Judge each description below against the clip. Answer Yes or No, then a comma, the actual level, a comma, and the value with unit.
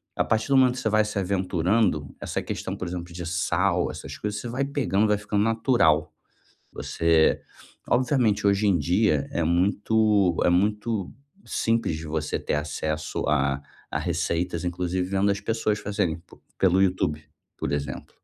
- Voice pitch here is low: Yes, very low, 95 Hz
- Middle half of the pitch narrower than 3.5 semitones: No, average, 4.2 semitones